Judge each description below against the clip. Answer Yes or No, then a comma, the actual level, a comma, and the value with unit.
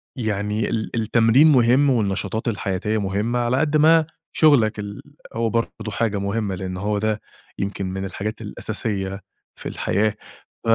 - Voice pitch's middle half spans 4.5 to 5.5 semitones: No, average, 2.8 semitones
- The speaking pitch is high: No, low, 110 Hz